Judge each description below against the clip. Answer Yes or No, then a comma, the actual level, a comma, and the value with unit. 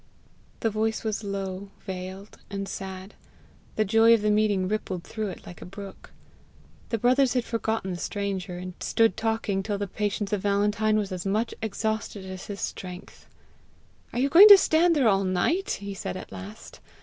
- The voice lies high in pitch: Yes, high, 205 Hz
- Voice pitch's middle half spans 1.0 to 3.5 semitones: Yes, narrow, 2.6 semitones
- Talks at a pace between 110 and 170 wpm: No, average, 180 wpm